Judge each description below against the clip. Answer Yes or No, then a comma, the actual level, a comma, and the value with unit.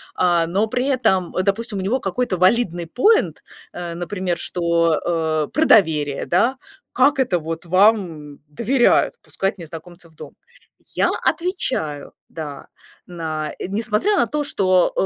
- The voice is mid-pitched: Yes, medium, 180 Hz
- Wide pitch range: Yes, wide, 5.8 semitones